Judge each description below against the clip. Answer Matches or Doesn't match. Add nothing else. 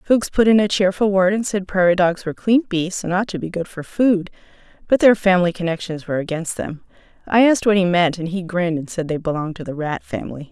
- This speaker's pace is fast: Matches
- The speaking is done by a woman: Matches